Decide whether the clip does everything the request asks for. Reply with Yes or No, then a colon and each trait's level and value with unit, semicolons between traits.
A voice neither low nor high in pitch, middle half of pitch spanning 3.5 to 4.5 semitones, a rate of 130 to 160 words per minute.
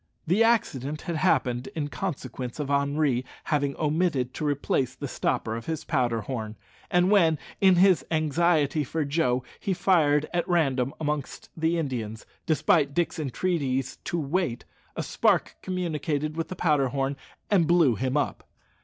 Yes: medium, 150 Hz; average, 4.2 semitones; average, 155 wpm